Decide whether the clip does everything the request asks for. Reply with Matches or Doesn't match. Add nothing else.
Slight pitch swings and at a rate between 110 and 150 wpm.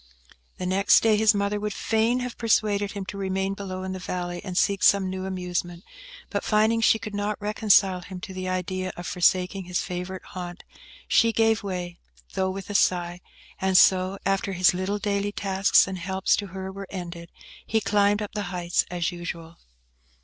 Doesn't match